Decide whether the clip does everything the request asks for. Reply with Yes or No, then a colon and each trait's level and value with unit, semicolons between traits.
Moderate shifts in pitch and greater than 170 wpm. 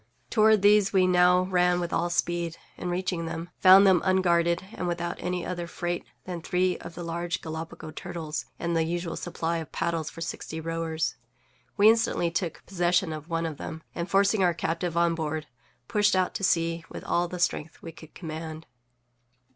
No: narrow, 1.6 semitones; average, 185 wpm